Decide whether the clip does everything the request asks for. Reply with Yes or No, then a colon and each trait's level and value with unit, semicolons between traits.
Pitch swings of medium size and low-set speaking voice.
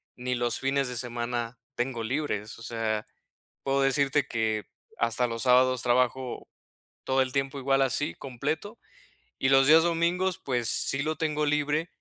Yes: average, 3.2 semitones; low, 130 Hz